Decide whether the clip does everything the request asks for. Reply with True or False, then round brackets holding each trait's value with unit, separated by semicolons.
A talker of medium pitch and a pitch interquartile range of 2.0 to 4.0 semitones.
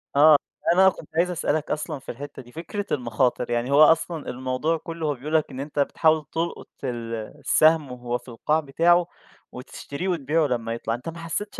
False (150 Hz; 4.5 semitones)